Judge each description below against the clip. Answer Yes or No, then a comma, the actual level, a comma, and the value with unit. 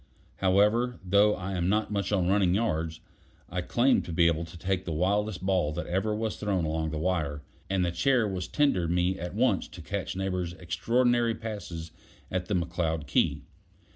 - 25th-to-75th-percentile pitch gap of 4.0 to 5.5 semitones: No, average, 3.5 semitones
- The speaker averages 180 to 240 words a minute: Yes, average, 185 wpm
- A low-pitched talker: Yes, very low, 95 Hz